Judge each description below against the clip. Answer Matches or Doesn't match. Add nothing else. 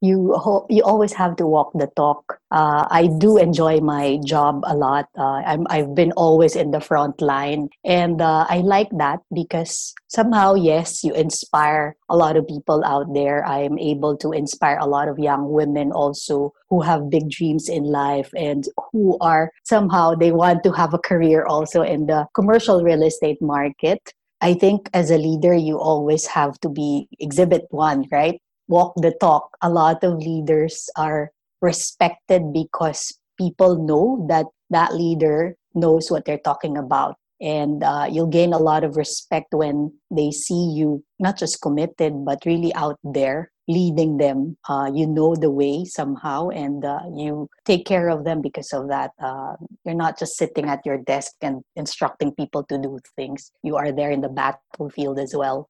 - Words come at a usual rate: Matches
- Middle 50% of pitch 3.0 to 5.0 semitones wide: Doesn't match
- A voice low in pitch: Doesn't match